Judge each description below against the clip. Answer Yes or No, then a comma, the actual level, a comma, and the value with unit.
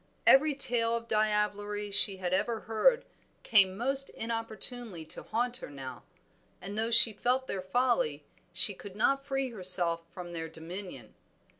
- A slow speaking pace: No, average, 150 wpm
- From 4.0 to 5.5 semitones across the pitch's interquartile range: Yes, average, 4.7 semitones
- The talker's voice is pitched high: Yes, high, 215 Hz